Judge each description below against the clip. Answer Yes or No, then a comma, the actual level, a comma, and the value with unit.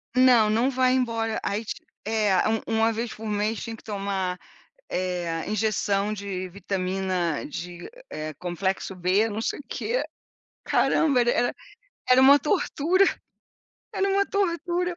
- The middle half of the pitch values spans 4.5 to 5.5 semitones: Yes, average, 5.0 semitones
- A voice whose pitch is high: Yes, high, 220 Hz